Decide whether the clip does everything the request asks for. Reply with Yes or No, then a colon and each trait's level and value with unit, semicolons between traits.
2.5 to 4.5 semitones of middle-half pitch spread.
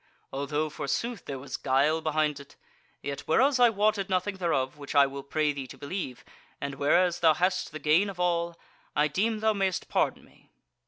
No: average, 5.0 semitones